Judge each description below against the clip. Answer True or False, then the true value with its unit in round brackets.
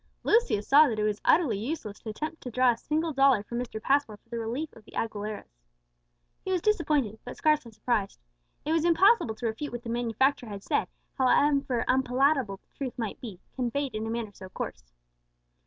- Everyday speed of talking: True (190 wpm)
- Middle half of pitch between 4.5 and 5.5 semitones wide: True (4.8 semitones)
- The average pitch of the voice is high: True (240 Hz)